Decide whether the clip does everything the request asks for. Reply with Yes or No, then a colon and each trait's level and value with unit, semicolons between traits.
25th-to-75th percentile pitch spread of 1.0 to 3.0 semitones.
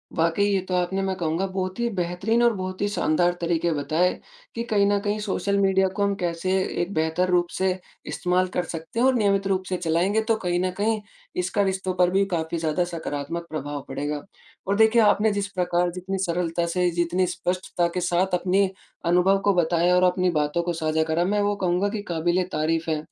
Yes: narrow, 2.5 semitones